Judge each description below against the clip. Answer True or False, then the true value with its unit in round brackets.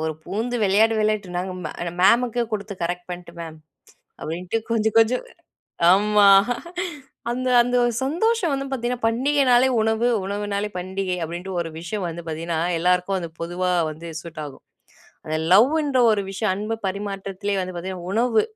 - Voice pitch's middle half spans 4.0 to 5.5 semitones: True (4.5 semitones)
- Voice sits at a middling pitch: False (200 Hz)